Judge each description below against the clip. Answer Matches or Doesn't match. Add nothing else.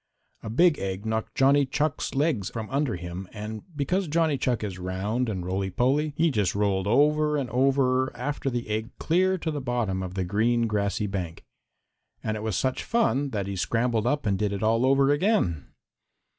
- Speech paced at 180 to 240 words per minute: Matches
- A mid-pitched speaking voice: Doesn't match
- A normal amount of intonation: Doesn't match